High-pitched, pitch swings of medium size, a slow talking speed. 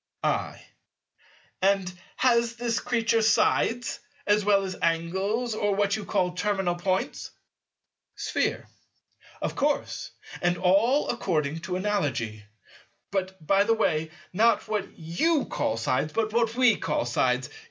Yes: high, 200 Hz; average, 4.3 semitones; slow, 130 wpm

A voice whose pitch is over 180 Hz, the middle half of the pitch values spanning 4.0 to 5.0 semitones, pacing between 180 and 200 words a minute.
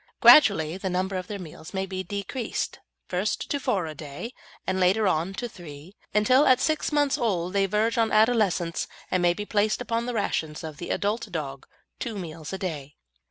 Yes: high, 190 Hz; average, 4.3 semitones; average, 195 wpm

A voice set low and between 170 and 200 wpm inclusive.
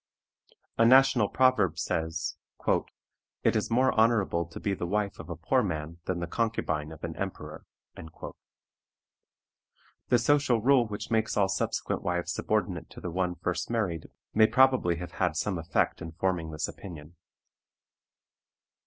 No: very low, 95 Hz; average, 145 wpm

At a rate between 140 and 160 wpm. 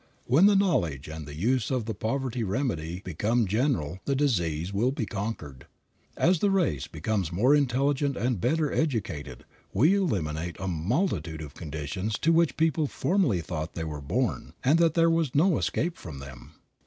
No: average, 170 wpm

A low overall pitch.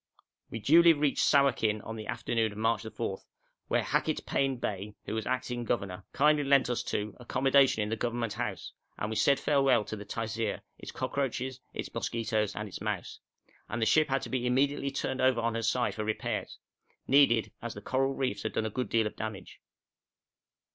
Yes: low, 120 Hz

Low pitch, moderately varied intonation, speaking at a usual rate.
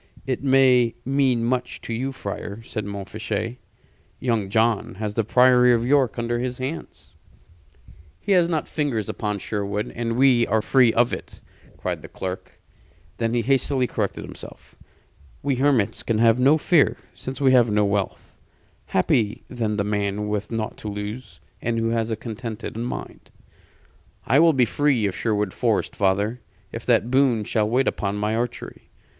Yes: low, 115 Hz; average, 3.4 semitones; average, 165 wpm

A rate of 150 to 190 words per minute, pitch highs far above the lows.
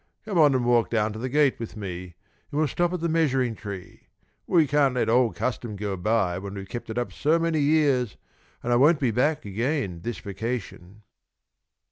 No: fast, 205 wpm; wide, 5.8 semitones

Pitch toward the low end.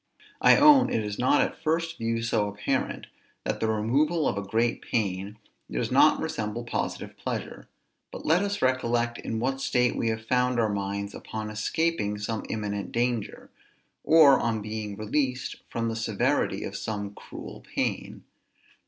Yes: low, 115 Hz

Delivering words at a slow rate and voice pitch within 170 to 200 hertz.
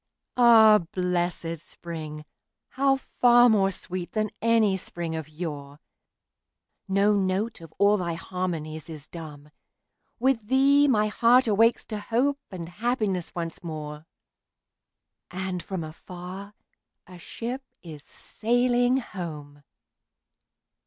Yes: slow, 110 wpm; high, 190 Hz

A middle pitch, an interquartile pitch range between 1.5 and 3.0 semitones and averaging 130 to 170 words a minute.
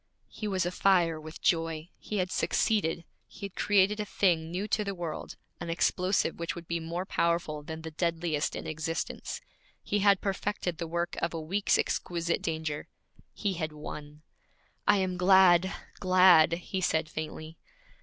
Yes: medium, 170 Hz; average, 2.7 semitones; average, 165 wpm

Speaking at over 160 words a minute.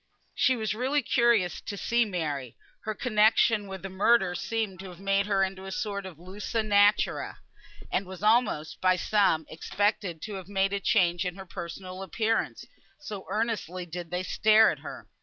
Yes: average, 175 wpm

